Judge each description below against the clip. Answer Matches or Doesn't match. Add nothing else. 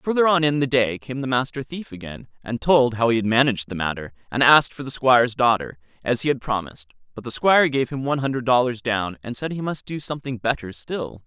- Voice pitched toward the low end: Matches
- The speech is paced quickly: Matches